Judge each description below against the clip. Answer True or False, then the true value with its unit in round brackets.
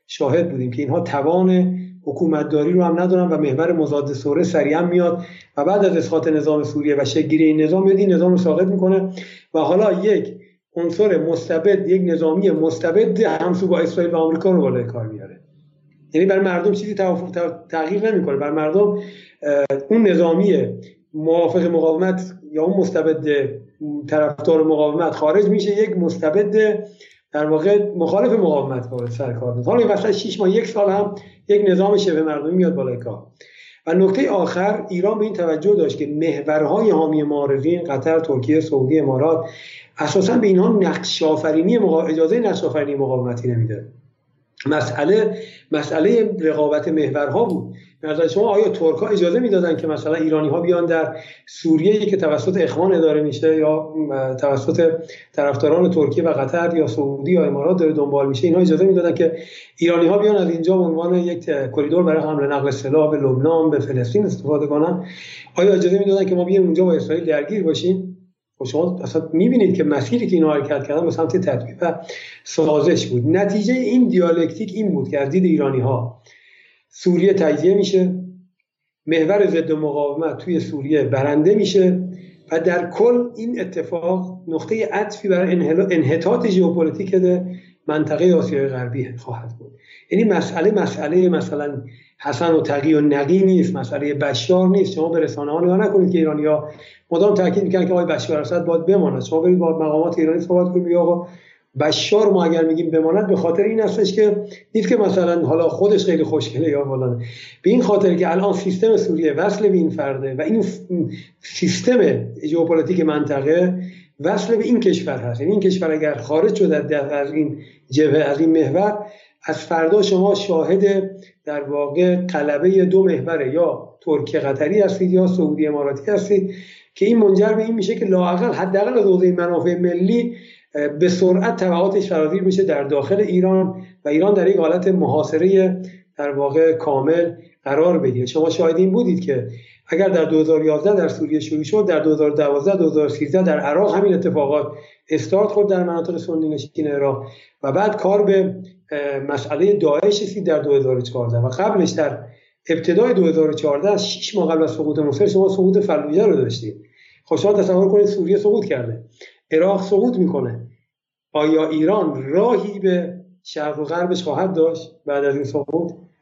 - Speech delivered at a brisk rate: True (160 wpm)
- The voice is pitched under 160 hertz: False (165 Hz)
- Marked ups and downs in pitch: False (3.9 semitones)